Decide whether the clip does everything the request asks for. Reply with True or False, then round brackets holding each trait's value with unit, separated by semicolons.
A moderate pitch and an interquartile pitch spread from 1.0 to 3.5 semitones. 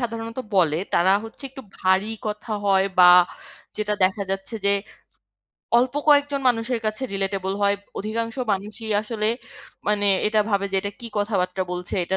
False (210 Hz; 2.9 semitones)